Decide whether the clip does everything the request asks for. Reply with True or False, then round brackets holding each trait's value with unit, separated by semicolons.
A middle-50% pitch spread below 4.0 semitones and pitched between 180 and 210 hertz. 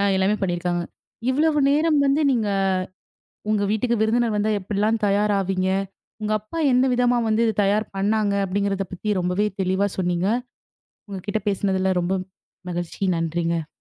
True (2.8 semitones; 200 Hz)